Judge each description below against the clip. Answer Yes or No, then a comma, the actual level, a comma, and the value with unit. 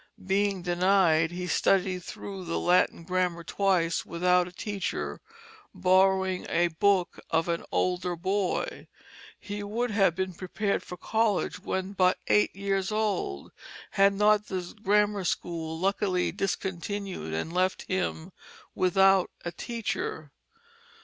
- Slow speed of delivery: Yes, slow, 125 wpm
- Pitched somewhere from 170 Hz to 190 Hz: Yes, medium, 185 Hz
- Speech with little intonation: Yes, narrow, 2.1 semitones